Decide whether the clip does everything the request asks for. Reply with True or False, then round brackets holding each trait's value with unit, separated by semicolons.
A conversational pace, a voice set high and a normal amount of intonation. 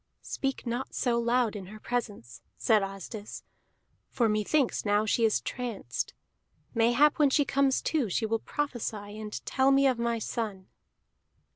True (150 wpm; 235 Hz; 3.6 semitones)